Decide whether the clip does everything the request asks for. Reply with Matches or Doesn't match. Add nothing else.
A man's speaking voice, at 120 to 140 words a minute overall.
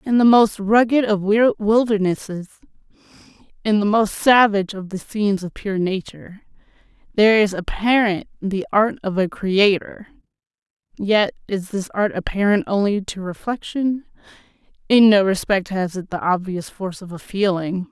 Doesn't match